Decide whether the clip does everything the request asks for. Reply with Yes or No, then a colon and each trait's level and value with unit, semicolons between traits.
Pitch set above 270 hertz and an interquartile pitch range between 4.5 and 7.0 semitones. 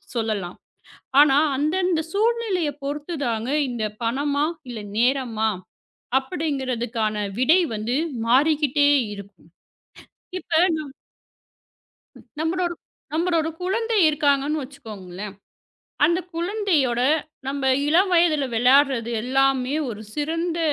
Yes: very high, 280 Hz; wide, 5.5 semitones